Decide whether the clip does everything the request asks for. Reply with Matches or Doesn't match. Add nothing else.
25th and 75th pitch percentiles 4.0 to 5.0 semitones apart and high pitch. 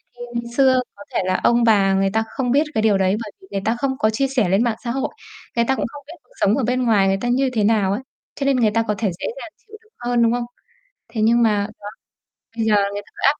Doesn't match